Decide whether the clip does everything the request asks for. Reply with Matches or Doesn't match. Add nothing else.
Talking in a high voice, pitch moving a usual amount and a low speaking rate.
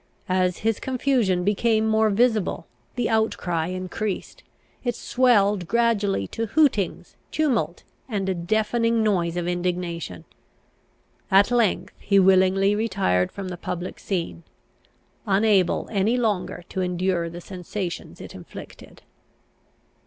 Matches